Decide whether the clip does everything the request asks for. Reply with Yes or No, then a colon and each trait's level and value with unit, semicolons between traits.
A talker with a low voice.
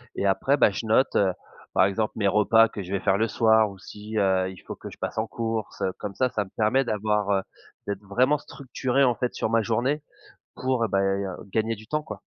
Yes: low, 110 Hz